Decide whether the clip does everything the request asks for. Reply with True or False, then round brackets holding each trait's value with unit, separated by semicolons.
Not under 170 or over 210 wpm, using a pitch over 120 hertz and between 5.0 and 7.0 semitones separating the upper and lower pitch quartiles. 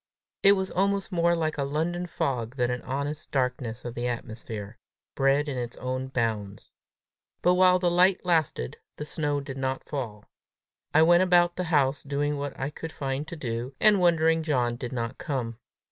True (180 wpm; 140 Hz; 5.3 semitones)